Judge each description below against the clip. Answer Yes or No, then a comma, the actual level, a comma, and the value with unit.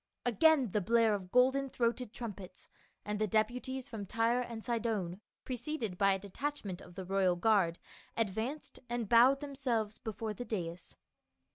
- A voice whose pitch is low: No, high, 225 Hz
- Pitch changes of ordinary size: Yes, average, 3.9 semitones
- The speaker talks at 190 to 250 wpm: No, average, 155 wpm